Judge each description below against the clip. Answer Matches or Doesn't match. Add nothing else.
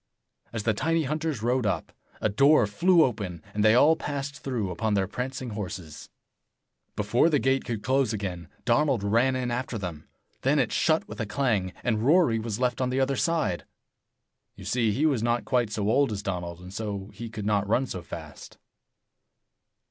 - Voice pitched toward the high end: Doesn't match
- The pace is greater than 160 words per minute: Matches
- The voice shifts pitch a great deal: Doesn't match